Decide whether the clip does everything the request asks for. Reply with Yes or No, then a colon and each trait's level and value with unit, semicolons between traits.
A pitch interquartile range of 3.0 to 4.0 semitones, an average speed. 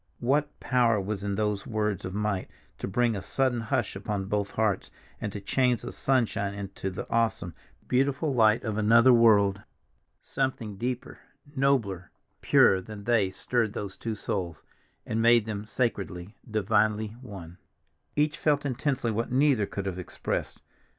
Yes: average, 3.5 semitones; average, 150 wpm